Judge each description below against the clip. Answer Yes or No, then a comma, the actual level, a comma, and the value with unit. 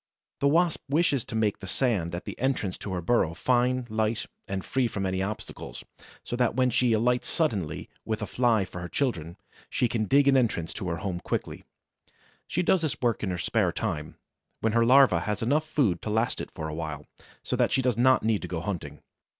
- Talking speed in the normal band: No, fast, 215 wpm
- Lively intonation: Yes, wide, 5.7 semitones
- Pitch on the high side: No, low, 110 Hz